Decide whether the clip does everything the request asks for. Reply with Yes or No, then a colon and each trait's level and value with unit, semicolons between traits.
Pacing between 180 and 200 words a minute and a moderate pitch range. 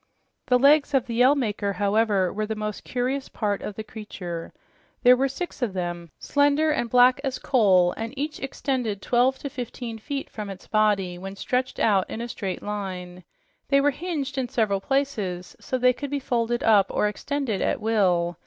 Yes: average, 190 wpm; average, 5.0 semitones